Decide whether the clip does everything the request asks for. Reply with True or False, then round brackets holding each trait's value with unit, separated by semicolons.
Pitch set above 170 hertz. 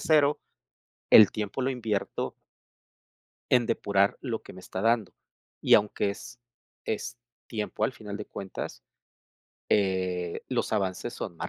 False (105 Hz)